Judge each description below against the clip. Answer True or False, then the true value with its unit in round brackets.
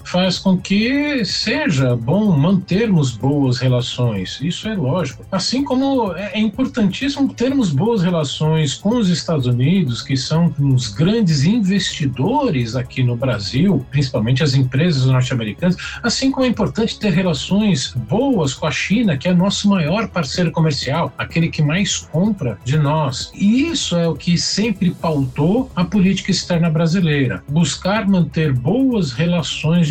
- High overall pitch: False (170 Hz)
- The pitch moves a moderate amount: False (6.4 semitones)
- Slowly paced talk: False (140 wpm)